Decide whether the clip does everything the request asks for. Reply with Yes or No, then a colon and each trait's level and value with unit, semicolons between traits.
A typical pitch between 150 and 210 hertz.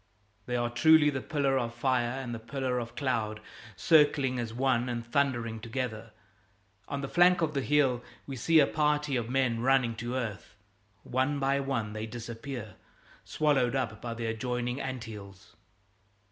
No: low, 125 Hz